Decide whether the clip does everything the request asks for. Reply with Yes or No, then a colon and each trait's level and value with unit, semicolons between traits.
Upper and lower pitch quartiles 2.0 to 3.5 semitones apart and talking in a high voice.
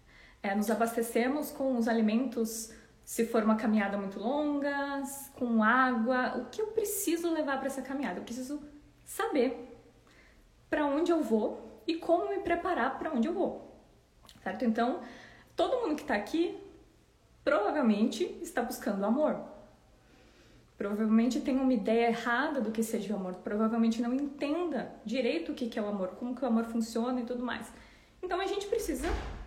No: average, 4.4 semitones; very high, 250 Hz